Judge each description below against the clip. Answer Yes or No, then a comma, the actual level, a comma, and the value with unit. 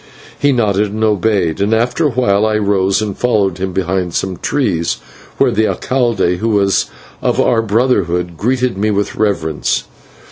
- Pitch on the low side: Yes, low, 105 Hz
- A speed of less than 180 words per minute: Yes, average, 165 wpm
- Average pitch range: Yes, average, 3.0 semitones